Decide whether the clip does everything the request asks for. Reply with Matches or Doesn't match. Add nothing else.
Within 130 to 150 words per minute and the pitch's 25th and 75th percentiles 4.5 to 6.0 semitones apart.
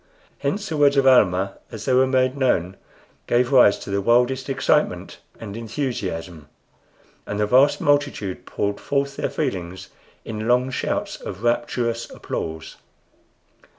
Matches